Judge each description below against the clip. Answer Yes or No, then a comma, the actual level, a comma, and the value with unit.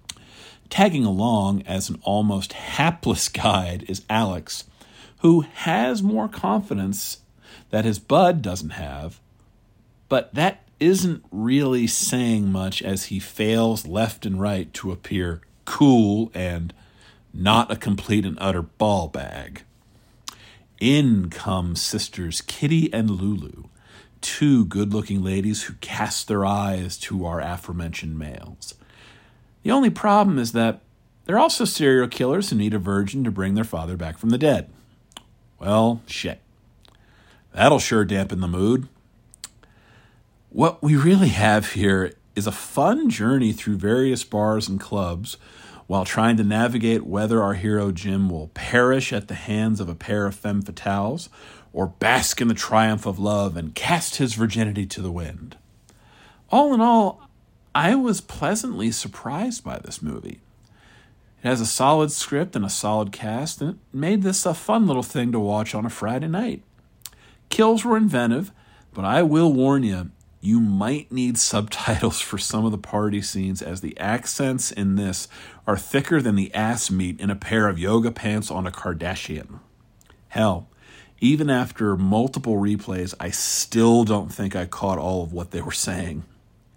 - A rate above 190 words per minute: No, average, 155 wpm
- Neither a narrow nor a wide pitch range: Yes, average, 3.9 semitones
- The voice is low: Yes, low, 110 Hz